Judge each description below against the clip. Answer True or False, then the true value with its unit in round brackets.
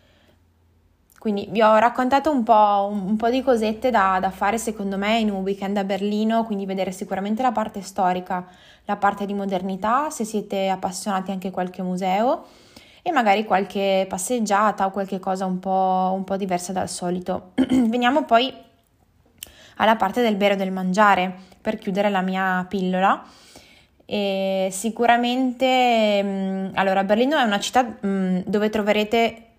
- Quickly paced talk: False (150 wpm)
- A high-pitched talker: True (200 Hz)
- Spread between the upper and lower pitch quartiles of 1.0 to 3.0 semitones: True (2.6 semitones)